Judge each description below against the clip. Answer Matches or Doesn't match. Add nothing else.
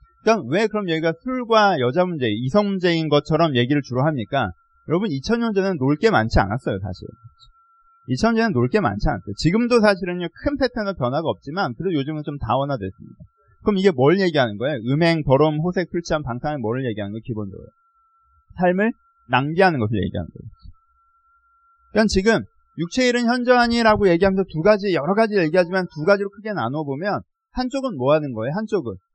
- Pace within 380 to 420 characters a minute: Matches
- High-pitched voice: Matches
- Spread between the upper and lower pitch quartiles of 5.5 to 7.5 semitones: Doesn't match